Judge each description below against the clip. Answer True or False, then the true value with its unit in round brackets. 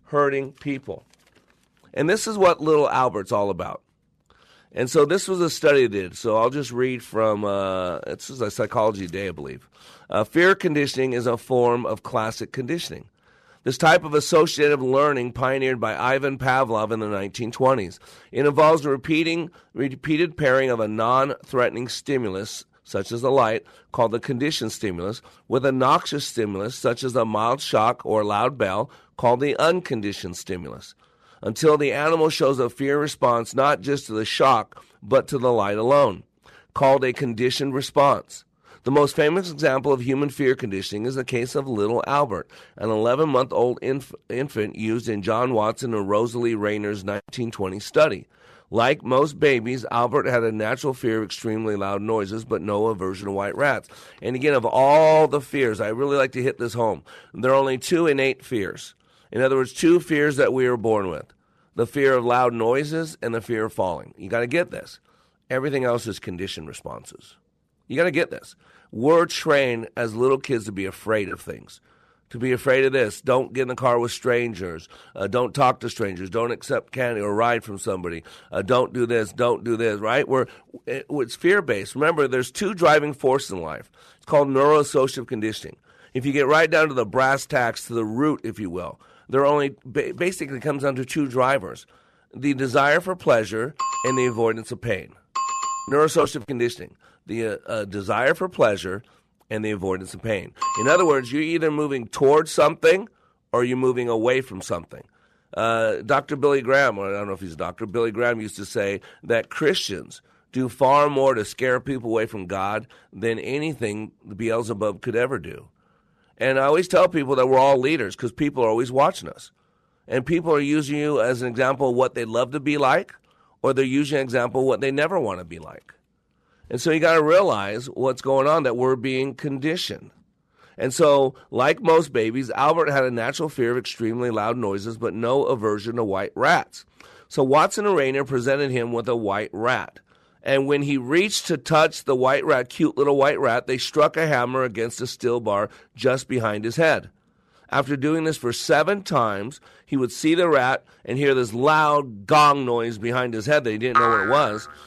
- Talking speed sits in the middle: True (190 wpm)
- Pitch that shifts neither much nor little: True (4.2 semitones)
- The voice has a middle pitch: False (130 Hz)